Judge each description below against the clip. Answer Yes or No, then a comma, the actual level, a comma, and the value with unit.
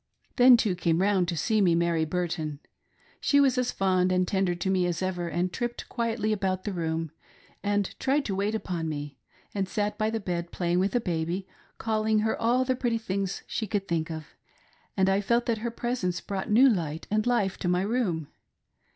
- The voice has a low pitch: No, high, 195 Hz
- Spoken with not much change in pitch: No, average, 4.1 semitones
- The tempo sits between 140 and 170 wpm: No, fast, 205 wpm